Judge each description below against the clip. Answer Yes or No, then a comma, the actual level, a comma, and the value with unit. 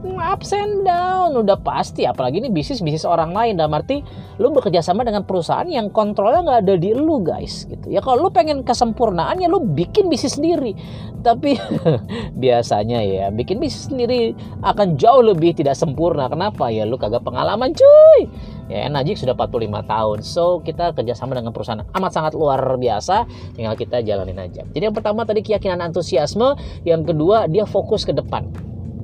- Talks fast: Yes, fast, 170 wpm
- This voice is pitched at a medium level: Yes, medium, 175 Hz